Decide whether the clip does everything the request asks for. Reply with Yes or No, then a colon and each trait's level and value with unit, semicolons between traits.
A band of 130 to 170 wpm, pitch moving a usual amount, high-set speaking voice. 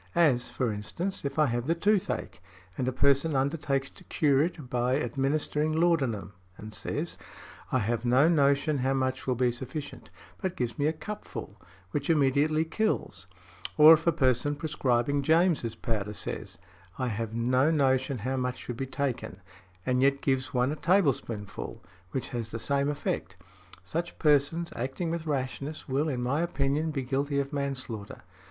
No: average, 165 wpm; average, 3.6 semitones; low, 135 Hz